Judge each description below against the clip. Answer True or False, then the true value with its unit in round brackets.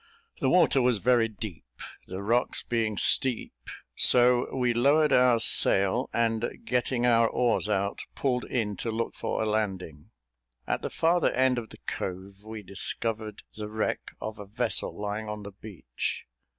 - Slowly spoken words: False (160 wpm)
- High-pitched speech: False (110 Hz)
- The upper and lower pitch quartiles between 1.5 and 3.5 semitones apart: True (3.2 semitones)